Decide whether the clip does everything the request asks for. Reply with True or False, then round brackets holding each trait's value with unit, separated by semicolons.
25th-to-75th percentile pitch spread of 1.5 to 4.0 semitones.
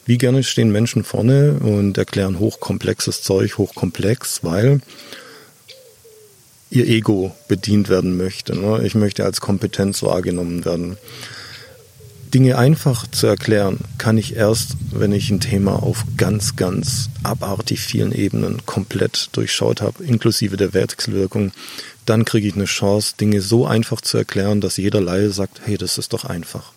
True (3.2 semitones)